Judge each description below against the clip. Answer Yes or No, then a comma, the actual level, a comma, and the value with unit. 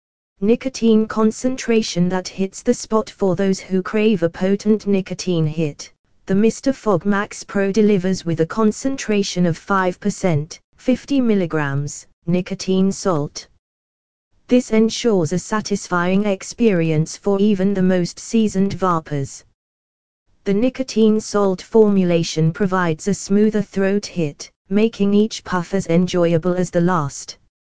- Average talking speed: No, slow, 120 wpm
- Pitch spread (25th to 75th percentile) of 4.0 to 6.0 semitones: No, average, 3.6 semitones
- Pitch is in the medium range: No, high, 195 Hz